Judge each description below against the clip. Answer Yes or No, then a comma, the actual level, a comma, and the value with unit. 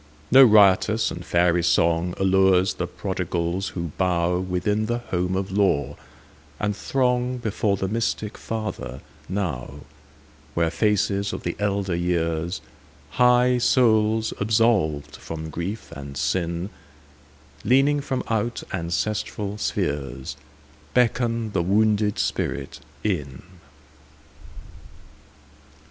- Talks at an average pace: No, slow, 90 wpm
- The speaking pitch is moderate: No, very low, 95 Hz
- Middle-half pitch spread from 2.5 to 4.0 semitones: No, average, 5.2 semitones